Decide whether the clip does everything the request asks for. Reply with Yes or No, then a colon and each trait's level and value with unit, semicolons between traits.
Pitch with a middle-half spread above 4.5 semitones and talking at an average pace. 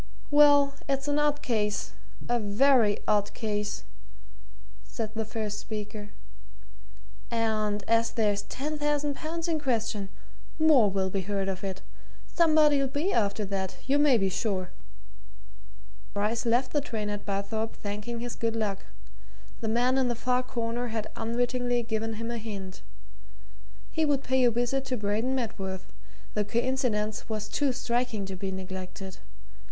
No: average, 3.9 semitones; average, 145 wpm